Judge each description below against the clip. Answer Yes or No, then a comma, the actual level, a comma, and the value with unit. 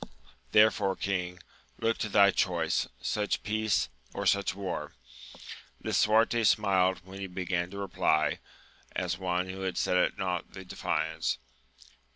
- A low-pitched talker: Yes, very low, 95 Hz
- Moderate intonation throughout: No, narrow, 2.0 semitones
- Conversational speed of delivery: No, slow, 130 wpm